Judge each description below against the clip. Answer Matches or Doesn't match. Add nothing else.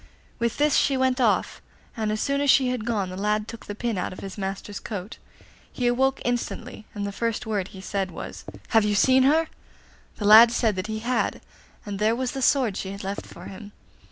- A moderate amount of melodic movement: Matches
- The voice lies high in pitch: Matches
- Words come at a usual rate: Doesn't match